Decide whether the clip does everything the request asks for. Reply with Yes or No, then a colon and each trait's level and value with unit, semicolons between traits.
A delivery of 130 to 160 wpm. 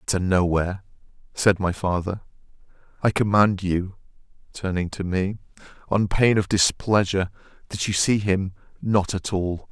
Yes: slow, 135 wpm